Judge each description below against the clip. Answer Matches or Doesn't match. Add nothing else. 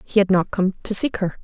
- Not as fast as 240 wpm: Doesn't match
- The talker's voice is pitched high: Matches